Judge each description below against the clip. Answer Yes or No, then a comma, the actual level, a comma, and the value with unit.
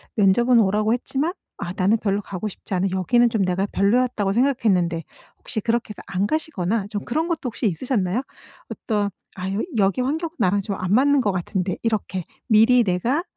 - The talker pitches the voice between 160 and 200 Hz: No, high, 210 Hz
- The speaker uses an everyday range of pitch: Yes, average, 4.4 semitones